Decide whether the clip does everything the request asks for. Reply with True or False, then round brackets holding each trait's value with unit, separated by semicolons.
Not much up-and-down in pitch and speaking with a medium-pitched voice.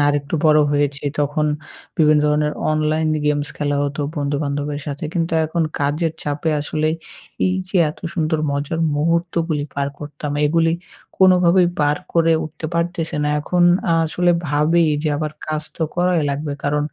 True (2.2 semitones; 155 Hz)